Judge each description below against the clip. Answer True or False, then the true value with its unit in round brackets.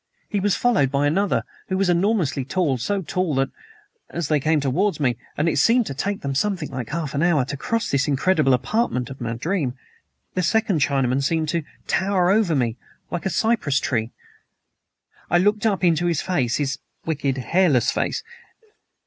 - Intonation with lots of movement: True (5.8 semitones)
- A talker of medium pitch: True (160 Hz)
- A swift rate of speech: False (185 wpm)